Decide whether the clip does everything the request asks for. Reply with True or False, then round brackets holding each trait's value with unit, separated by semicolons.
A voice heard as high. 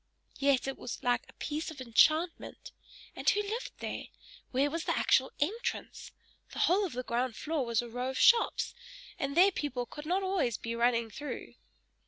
True (280 Hz)